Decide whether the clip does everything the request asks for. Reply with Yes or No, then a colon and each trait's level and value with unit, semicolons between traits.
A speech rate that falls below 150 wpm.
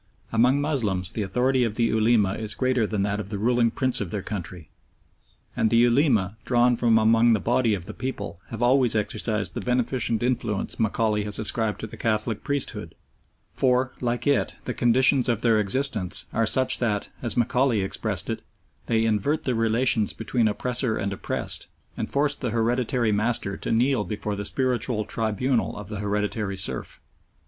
No: average, 175 wpm